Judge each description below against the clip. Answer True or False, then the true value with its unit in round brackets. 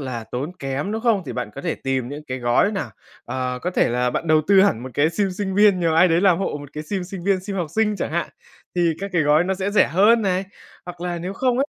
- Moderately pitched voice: True (175 Hz)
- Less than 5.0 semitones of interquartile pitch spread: False (5.3 semitones)